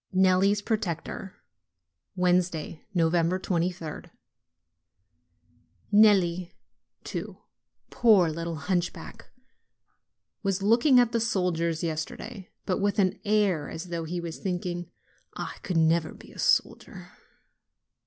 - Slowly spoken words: Yes, slow, 100 wpm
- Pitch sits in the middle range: Yes, medium, 180 Hz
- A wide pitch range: No, average, 2.9 semitones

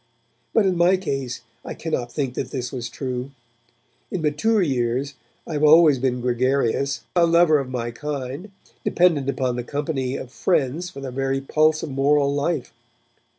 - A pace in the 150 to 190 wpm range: Yes, average, 165 wpm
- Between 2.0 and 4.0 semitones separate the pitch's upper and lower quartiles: Yes, average, 3.6 semitones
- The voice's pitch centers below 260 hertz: Yes, medium, 140 Hz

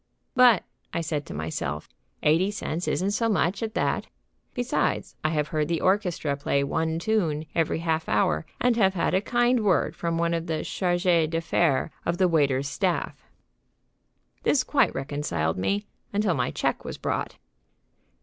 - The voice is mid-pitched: Yes, medium, 170 Hz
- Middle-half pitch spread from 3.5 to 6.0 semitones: Yes, average, 5.0 semitones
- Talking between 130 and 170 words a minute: Yes, average, 160 wpm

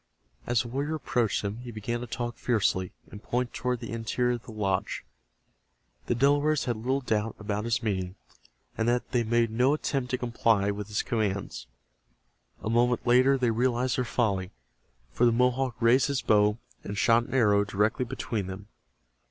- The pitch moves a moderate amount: Yes, average, 3.0 semitones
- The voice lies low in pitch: Yes, low, 120 Hz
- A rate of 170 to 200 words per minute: Yes, average, 175 wpm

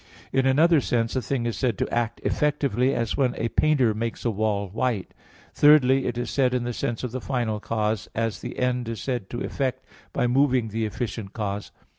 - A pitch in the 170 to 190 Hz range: No, low, 120 Hz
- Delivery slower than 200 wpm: No, fast, 205 wpm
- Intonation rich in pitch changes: No, average, 2.8 semitones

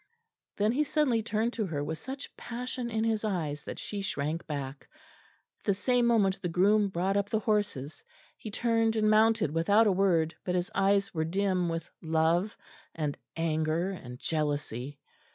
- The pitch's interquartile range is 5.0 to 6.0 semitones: Yes, average, 5.3 semitones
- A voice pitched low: No, high, 195 Hz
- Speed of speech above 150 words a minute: Yes, average, 170 wpm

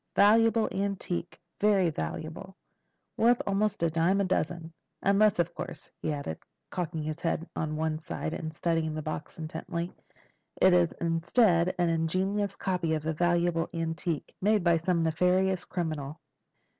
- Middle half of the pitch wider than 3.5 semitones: No, average, 2.9 semitones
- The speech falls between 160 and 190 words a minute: No, average, 145 wpm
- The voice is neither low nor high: Yes, medium, 170 Hz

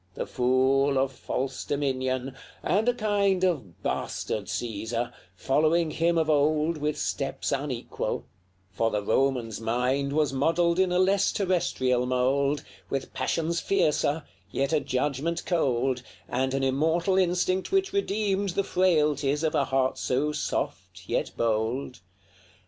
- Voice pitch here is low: No, medium, 145 Hz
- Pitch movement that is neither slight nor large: Yes, average, 4.8 semitones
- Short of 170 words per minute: Yes, slow, 135 wpm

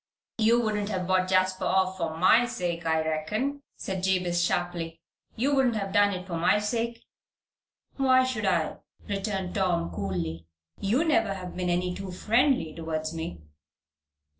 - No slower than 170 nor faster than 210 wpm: No, average, 155 wpm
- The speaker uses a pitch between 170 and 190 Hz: Yes, medium, 185 Hz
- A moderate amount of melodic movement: Yes, average, 4.2 semitones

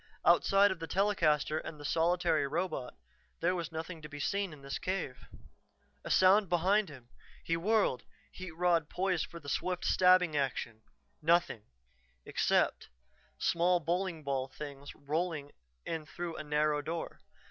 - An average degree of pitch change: Yes, average, 3.5 semitones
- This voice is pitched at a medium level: Yes, medium, 165 Hz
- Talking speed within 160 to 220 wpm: No, average, 145 wpm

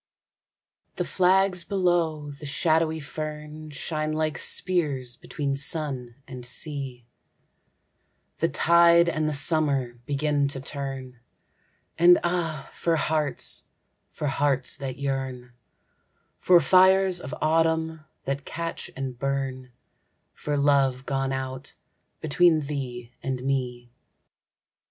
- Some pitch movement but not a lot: Yes, average, 3.3 semitones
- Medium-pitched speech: Yes, medium, 145 Hz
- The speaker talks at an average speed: No, slow, 110 wpm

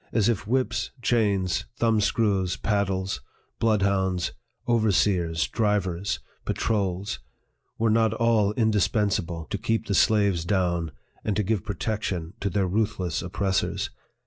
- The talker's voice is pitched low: Yes, low, 100 Hz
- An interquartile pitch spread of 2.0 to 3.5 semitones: Yes, average, 2.9 semitones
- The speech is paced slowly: Yes, slow, 120 wpm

